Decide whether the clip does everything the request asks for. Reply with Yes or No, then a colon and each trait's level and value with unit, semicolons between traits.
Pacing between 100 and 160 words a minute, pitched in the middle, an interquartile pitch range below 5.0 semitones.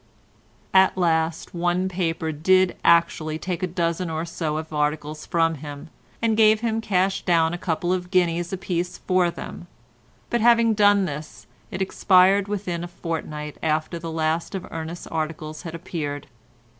Yes: average, 155 wpm; medium, 170 Hz; average, 2.8 semitones